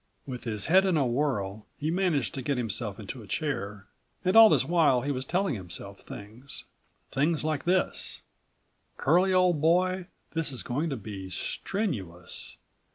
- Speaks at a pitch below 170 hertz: Yes, medium, 140 Hz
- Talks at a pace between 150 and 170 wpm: Yes, average, 160 wpm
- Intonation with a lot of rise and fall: Yes, wide, 7.9 semitones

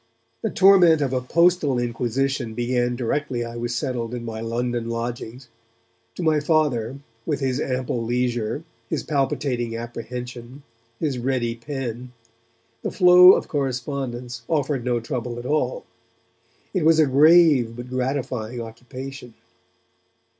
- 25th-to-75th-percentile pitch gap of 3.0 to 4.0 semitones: Yes, average, 3.3 semitones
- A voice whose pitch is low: Yes, low, 125 Hz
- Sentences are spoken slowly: Yes, slow, 130 wpm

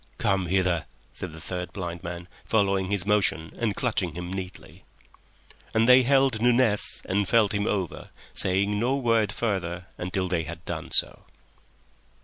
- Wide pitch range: No, average, 3.8 semitones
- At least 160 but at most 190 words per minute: No, average, 150 wpm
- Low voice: Yes, very low, 95 Hz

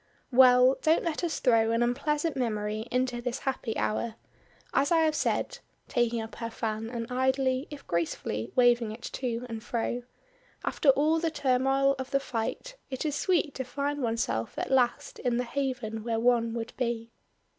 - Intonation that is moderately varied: Yes, average, 3.1 semitones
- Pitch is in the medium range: No, very high, 250 Hz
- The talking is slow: No, average, 175 wpm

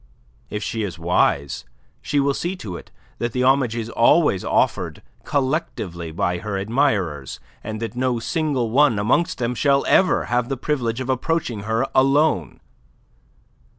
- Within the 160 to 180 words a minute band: No, average, 150 wpm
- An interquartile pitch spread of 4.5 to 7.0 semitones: Yes, average, 5.1 semitones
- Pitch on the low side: Yes, low, 120 Hz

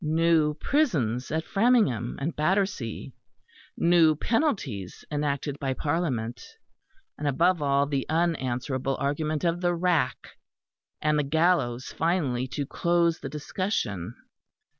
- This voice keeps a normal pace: No, slow, 115 wpm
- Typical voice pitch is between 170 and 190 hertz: No, medium, 150 Hz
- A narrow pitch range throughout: No, average, 4.3 semitones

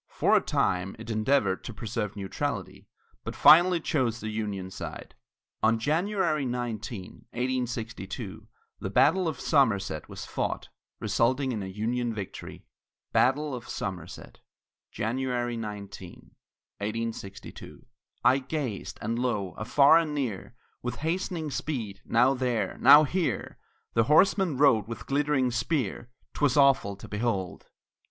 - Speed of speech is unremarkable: No, slow, 125 wpm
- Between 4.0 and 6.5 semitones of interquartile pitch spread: Yes, average, 4.9 semitones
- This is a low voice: Yes, low, 120 Hz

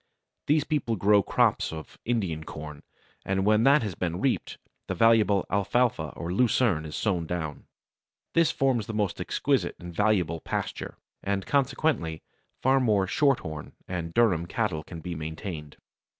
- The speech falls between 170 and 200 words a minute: No, average, 150 wpm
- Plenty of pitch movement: Yes, wide, 6.1 semitones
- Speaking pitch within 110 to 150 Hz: No, very low, 95 Hz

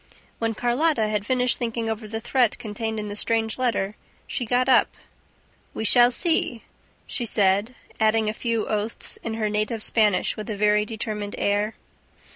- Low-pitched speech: No, high, 220 Hz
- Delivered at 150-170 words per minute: Yes, average, 165 wpm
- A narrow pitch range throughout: Yes, narrow, 2.2 semitones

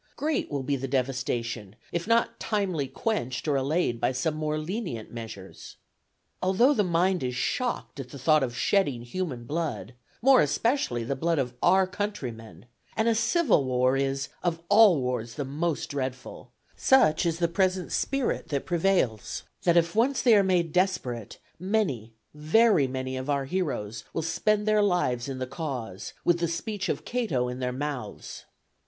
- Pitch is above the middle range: No, medium, 155 Hz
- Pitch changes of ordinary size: No, wide, 6.9 semitones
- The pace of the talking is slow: No, average, 170 wpm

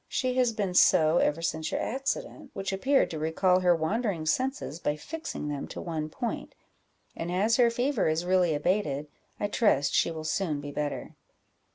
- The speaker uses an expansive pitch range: Yes, wide, 6.5 semitones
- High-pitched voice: No, medium, 180 Hz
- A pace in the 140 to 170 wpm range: No, average, 180 wpm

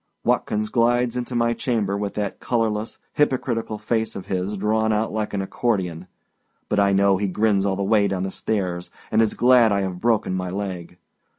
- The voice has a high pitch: No, low, 105 Hz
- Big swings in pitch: No, average, 2.7 semitones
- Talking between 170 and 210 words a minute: Yes, average, 190 wpm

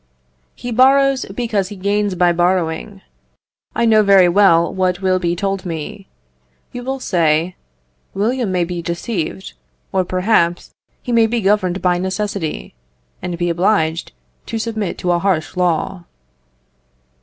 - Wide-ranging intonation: No, average, 3.4 semitones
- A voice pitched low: No, high, 190 Hz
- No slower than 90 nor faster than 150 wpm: Yes, average, 140 wpm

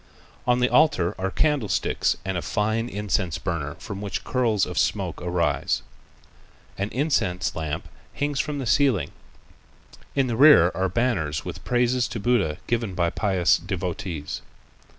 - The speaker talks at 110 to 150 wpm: Yes, average, 145 wpm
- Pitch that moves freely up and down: Yes, wide, 5.7 semitones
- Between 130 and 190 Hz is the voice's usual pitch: No, low, 105 Hz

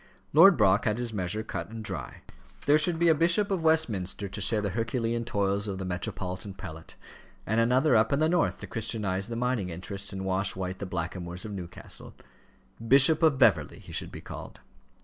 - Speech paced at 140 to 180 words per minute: No, average, 195 wpm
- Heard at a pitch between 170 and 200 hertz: No, low, 105 Hz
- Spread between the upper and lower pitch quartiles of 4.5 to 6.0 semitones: Yes, average, 5.2 semitones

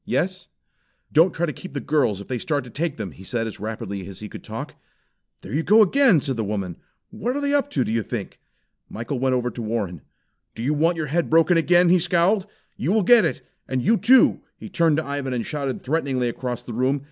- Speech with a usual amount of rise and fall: No, wide, 6.7 semitones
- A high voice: No, medium, 145 Hz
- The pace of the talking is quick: Yes, fast, 235 wpm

